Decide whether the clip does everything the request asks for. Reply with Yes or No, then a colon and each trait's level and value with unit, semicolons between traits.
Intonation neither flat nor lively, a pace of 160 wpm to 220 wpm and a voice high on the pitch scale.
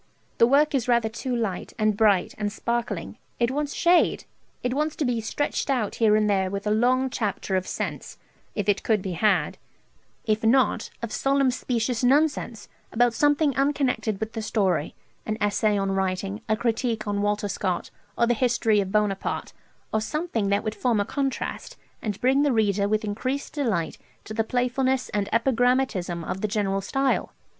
Yes: average, 3.8 semitones; average, 180 wpm; high, 225 Hz